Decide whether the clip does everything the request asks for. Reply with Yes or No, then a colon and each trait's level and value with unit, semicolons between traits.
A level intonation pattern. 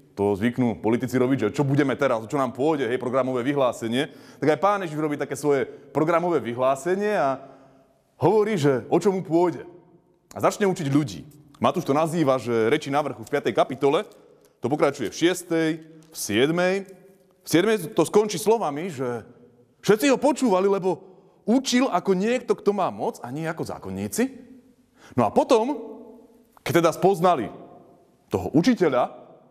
No: wide, 6.4 semitones